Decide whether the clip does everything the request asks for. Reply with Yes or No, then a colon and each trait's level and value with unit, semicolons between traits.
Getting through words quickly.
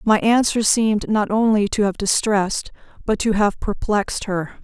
No: average, 170 wpm